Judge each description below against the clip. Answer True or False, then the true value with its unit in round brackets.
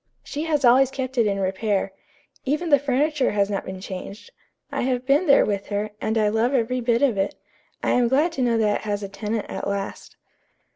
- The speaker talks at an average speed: False (220 wpm)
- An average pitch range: True (4.7 semitones)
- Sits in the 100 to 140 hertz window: False (230 Hz)